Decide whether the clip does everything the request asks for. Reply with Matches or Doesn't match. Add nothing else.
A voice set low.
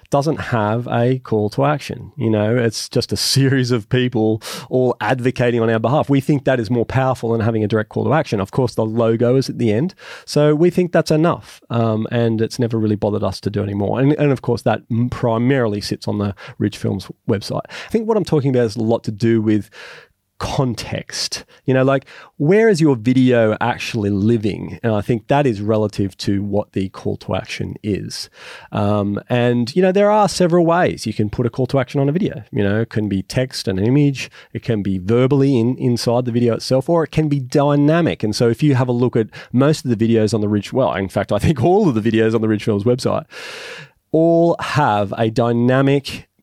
Matches